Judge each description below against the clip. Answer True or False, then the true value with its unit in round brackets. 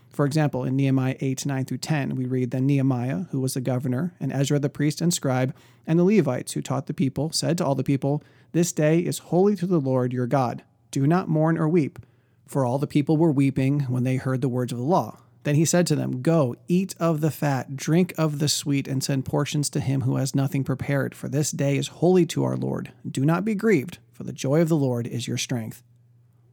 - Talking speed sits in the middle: False (235 wpm)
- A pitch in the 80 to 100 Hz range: False (140 Hz)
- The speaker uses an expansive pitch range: False (3.5 semitones)